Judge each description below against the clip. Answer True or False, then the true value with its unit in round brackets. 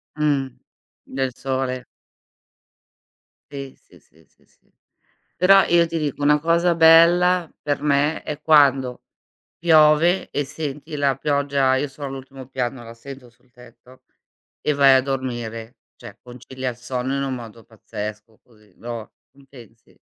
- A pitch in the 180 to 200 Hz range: False (135 Hz)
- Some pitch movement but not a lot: True (3.3 semitones)